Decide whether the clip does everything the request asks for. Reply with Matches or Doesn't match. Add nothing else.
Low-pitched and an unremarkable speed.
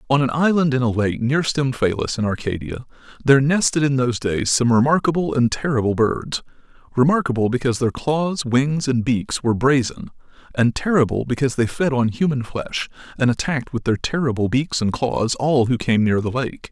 Matches